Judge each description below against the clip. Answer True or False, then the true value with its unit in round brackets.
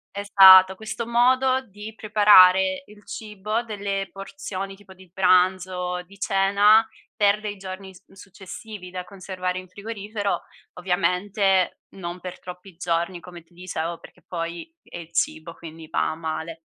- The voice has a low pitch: False (190 Hz)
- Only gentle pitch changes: True (2.3 semitones)